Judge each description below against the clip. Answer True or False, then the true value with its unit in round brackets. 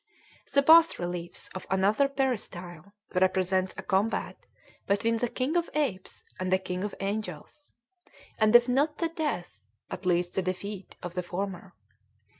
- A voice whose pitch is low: False (195 Hz)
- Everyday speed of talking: True (150 wpm)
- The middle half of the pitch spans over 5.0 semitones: True (5.4 semitones)